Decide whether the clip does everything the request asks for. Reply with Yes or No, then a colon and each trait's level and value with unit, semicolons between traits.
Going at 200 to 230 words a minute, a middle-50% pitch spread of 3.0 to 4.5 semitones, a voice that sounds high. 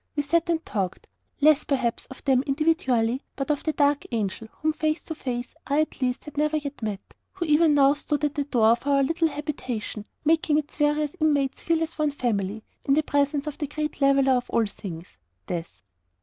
Yes: fast, 205 wpm; average, 3.6 semitones; very high, 285 Hz